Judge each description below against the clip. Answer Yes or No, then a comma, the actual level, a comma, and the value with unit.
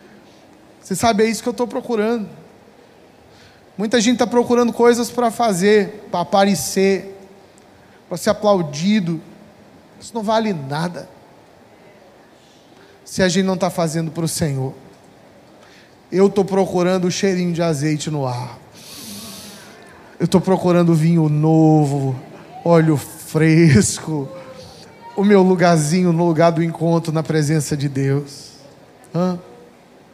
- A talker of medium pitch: Yes, medium, 175 Hz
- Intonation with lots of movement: No, average, 4.0 semitones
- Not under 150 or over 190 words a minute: No, average, 125 wpm